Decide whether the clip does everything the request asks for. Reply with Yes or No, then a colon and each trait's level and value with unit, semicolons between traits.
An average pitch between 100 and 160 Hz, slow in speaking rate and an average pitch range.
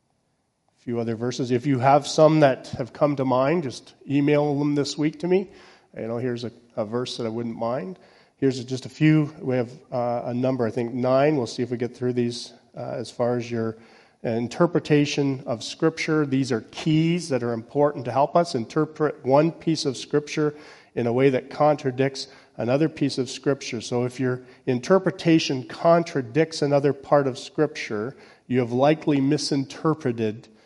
No: low, 135 Hz; average, 180 wpm; average, 3.6 semitones